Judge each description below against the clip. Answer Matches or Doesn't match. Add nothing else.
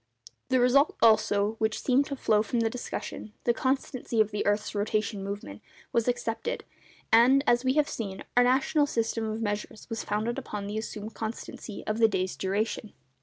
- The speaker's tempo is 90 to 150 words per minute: Doesn't match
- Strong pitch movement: Doesn't match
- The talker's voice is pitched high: Matches